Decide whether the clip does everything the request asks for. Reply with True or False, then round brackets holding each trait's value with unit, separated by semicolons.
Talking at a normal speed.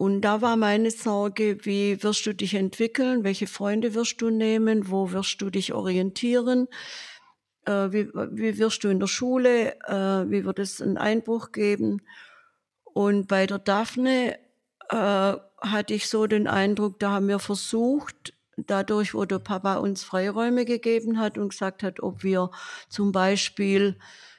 True (155 wpm)